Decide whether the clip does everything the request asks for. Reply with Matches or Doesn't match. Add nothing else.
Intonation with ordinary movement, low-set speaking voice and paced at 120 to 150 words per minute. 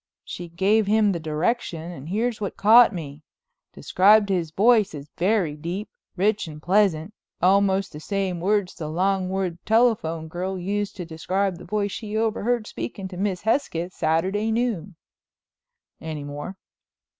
Doesn't match